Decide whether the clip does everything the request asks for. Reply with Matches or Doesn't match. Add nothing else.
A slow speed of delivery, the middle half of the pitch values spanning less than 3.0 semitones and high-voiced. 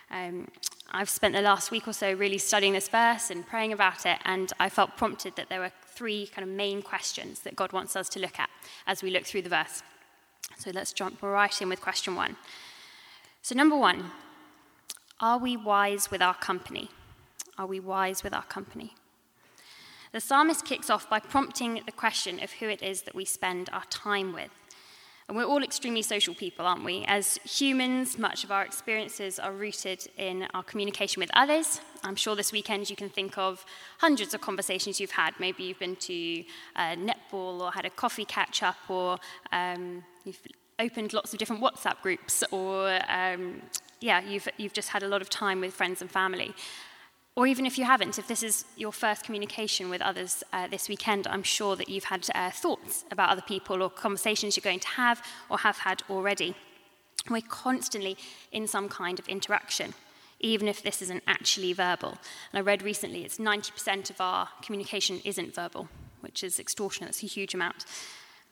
Doesn't match